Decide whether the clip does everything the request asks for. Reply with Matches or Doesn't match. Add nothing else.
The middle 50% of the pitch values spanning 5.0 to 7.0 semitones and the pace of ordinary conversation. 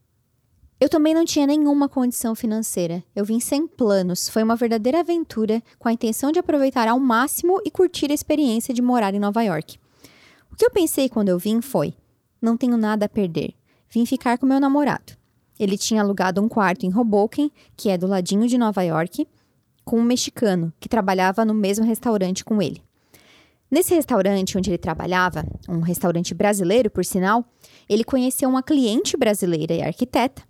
Matches